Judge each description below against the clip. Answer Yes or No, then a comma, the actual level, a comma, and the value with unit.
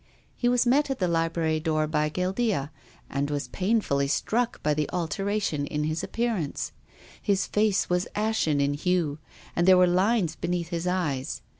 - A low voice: No, medium, 175 Hz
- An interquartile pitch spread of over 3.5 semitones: Yes, average, 5.1 semitones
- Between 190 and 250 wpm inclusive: No, average, 170 wpm